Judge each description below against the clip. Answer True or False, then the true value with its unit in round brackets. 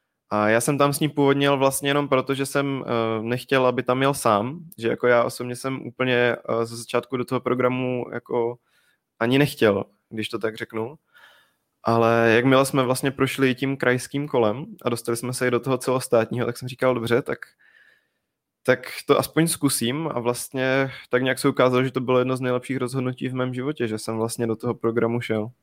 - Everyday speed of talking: False (195 wpm)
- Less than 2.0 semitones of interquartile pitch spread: False (2.4 semitones)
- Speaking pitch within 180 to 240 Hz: False (125 Hz)